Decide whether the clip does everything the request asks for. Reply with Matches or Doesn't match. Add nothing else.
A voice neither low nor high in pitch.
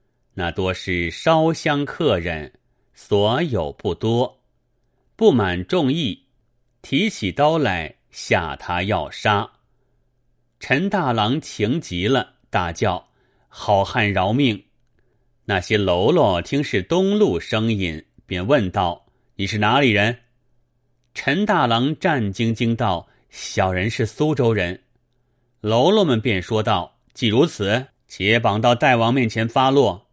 Doesn't match